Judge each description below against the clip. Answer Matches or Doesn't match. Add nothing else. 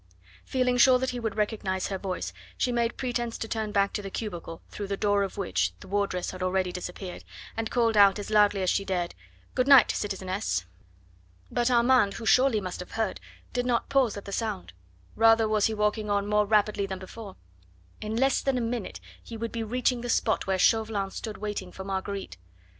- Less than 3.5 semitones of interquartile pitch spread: Matches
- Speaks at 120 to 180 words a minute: Doesn't match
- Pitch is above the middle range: Matches